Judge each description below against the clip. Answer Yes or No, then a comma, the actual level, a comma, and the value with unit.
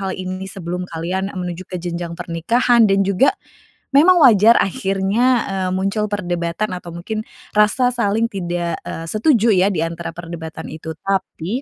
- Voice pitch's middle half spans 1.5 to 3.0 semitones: No, average, 3.8 semitones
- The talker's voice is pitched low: No, high, 190 Hz